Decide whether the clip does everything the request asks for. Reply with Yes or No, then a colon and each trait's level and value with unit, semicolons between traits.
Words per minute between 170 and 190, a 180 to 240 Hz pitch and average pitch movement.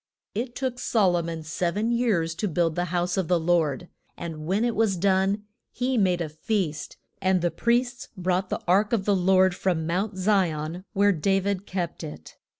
No: average, 200 wpm; medium, 185 Hz; average, 3.3 semitones